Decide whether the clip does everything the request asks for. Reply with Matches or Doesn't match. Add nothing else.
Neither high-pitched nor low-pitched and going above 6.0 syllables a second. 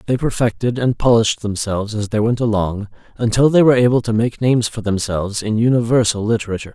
Doesn't match